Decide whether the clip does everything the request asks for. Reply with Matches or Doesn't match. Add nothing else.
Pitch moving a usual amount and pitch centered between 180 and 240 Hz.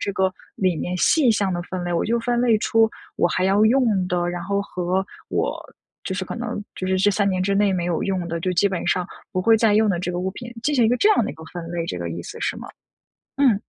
Matches